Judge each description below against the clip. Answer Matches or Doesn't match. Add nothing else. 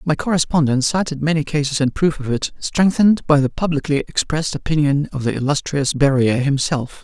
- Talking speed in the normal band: Matches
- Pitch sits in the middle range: Matches